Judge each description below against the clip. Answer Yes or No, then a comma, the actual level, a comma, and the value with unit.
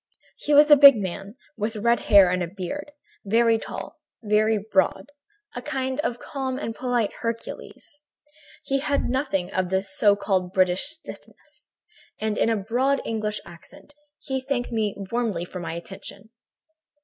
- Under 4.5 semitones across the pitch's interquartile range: No, average, 5.2 semitones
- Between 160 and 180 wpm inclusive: No, average, 150 wpm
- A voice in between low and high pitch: No, high, 220 Hz